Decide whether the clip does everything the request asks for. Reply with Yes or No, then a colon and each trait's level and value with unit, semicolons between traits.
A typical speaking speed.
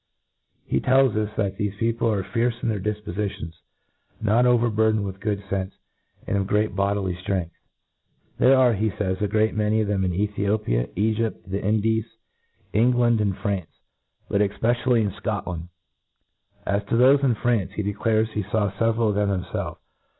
Yes: average, 170 wpm